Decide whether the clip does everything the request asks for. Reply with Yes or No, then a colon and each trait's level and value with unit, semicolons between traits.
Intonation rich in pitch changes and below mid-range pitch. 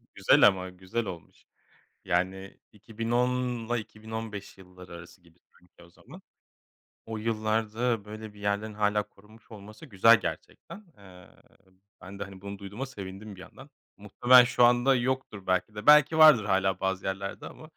No: average, 3.2 semitones; low, 105 Hz